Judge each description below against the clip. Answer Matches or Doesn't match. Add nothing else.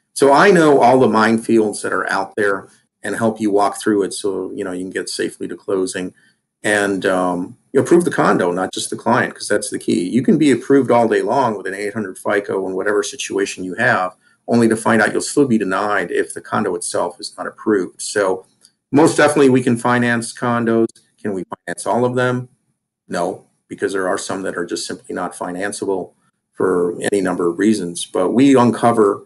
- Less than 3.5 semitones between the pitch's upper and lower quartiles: Doesn't match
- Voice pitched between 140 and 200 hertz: Doesn't match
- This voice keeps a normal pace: Doesn't match